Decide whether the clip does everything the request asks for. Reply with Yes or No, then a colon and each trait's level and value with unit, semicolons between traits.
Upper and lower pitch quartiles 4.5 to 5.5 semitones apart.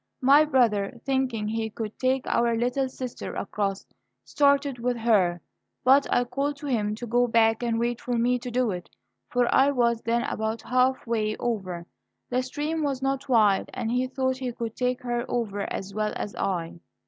No: average, 2.9 semitones